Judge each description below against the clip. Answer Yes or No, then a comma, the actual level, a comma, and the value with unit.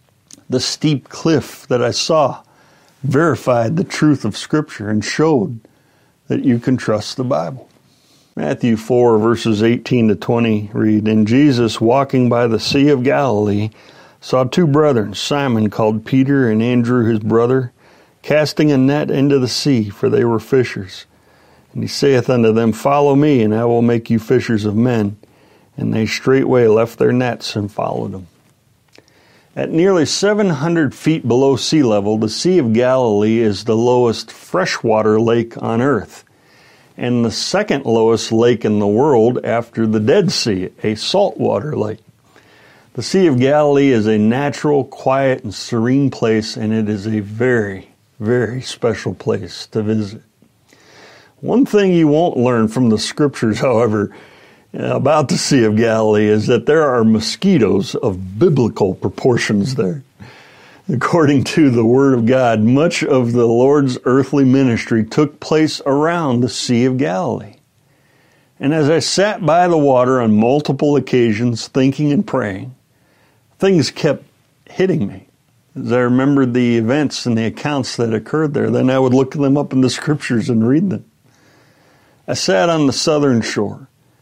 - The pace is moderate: Yes, average, 155 wpm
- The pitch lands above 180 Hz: No, low, 125 Hz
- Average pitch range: Yes, average, 4.0 semitones